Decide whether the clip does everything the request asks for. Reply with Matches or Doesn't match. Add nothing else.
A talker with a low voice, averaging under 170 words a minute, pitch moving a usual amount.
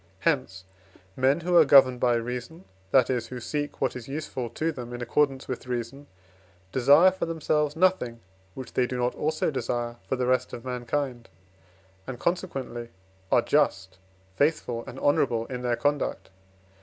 Matches